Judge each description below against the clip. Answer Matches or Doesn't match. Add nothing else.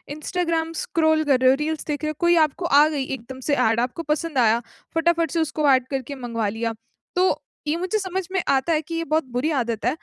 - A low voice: Doesn't match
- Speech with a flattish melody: Doesn't match